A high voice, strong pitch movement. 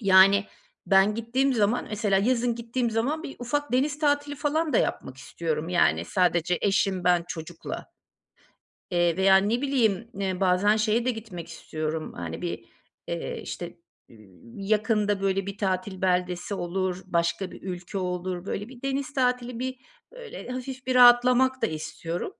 Yes: high, 205 Hz; wide, 5.7 semitones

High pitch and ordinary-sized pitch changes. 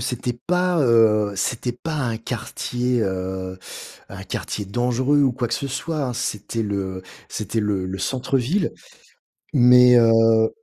No: low, 120 Hz; average, 3.2 semitones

